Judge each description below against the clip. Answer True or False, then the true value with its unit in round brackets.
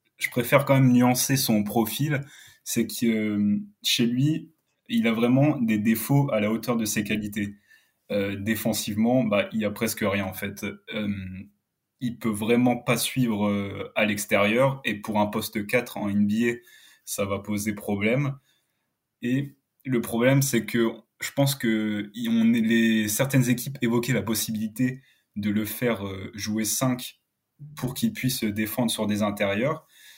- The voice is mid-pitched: False (115 Hz)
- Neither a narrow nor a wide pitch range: True (3.3 semitones)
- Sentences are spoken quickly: False (145 wpm)